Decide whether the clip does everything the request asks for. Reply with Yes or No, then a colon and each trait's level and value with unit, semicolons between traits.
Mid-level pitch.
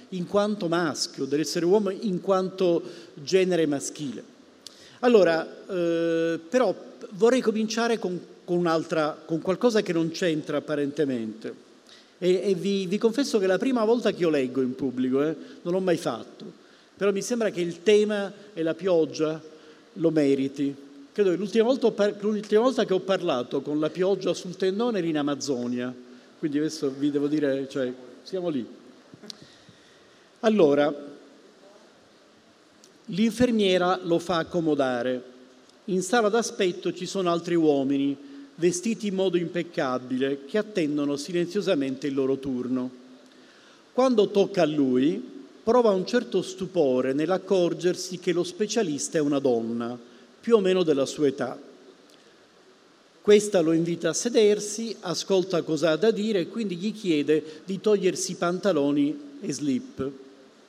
Yes: medium, 175 Hz